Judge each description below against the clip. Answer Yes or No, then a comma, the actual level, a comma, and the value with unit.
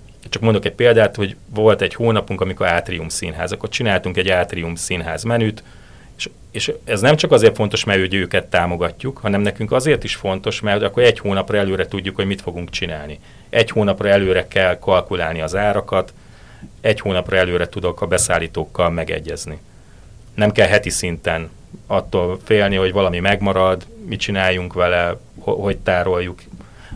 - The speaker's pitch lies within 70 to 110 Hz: Yes, very low, 95 Hz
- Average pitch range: Yes, average, 3.0 semitones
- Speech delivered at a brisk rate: Yes, fast, 160 wpm